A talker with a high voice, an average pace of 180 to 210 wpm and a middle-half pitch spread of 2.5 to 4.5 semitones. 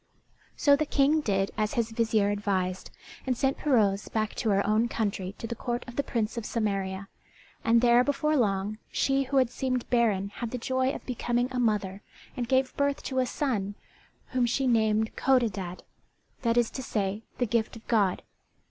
Yes: high, 230 Hz; average, 185 wpm; average, 3.7 semitones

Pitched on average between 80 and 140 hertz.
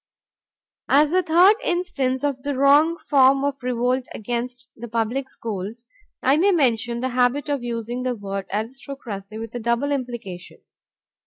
No: very high, 250 Hz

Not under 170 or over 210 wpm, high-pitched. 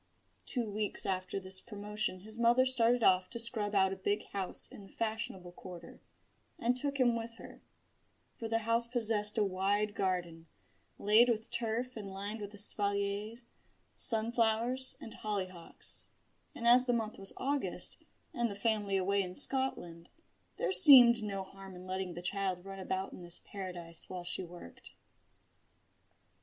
No: average, 155 wpm; high, 205 Hz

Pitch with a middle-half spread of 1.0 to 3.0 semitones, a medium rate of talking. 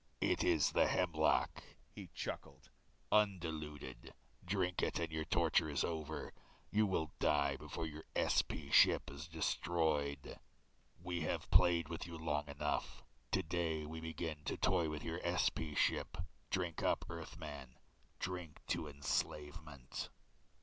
No: narrow, 2.4 semitones; slow, 130 wpm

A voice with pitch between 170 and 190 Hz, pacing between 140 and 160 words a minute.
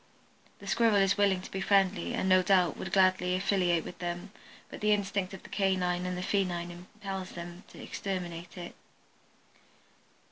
No: medium, 185 Hz; average, 170 wpm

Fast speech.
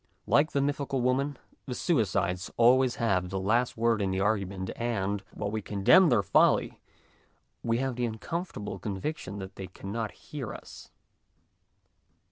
No: average, 165 wpm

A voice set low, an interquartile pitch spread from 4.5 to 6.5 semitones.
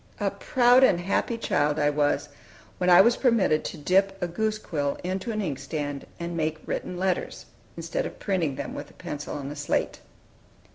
No: medium, 175 Hz; average, 5.2 semitones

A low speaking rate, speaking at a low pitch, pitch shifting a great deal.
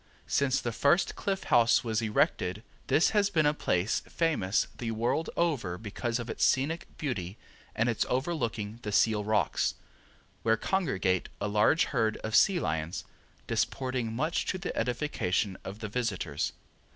No: average, 150 wpm; low, 115 Hz; wide, 5.9 semitones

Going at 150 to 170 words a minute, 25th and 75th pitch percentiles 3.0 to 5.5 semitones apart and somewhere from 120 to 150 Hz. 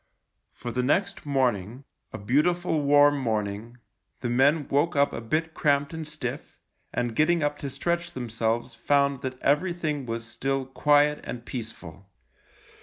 Yes: average, 155 wpm; average, 4.0 semitones; medium, 140 Hz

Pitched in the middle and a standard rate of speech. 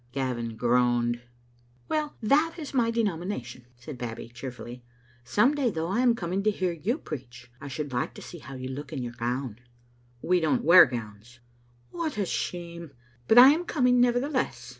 Yes: medium, 150 Hz; average, 180 wpm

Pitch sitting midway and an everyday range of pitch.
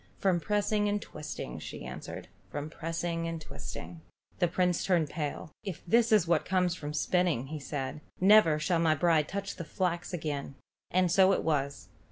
Yes: medium, 170 Hz; average, 3.3 semitones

